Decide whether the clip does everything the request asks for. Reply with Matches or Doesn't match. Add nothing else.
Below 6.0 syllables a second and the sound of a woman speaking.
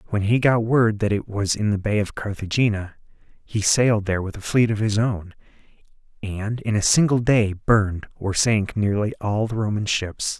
Doesn't match